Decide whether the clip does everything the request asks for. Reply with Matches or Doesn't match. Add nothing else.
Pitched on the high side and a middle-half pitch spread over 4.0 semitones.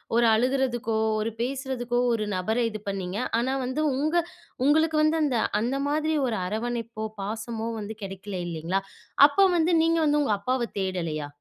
Matches